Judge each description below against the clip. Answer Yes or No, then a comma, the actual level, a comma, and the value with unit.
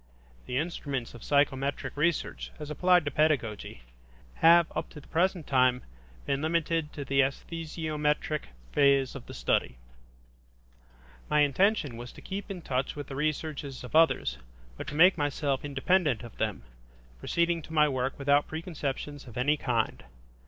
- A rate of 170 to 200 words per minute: No, average, 150 wpm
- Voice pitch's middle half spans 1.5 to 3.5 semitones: Yes, average, 3.2 semitones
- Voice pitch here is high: No, medium, 145 Hz